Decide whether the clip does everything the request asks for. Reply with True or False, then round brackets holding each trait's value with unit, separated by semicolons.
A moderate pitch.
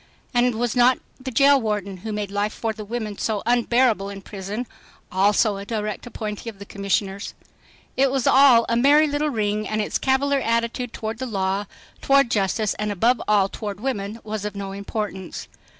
False (215 Hz)